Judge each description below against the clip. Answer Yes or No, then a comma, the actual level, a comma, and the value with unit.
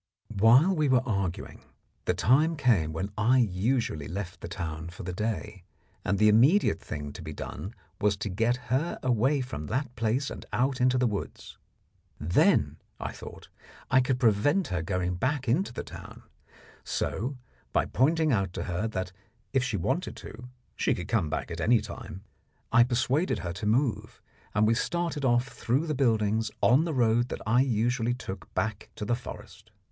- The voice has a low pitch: Yes, low, 115 Hz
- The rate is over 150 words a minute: Yes, average, 180 wpm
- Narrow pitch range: No, average, 5.1 semitones